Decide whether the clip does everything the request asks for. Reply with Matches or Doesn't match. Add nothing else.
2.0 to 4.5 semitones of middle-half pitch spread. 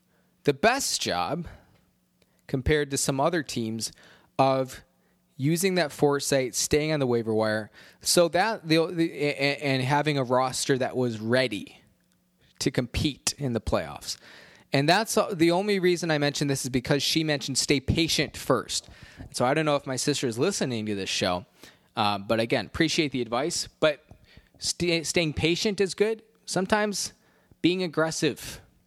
Doesn't match